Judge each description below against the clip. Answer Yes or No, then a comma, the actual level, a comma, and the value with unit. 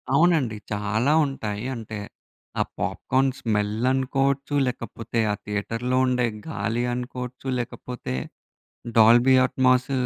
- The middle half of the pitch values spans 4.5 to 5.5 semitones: No, average, 2.9 semitones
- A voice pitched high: No, low, 125 Hz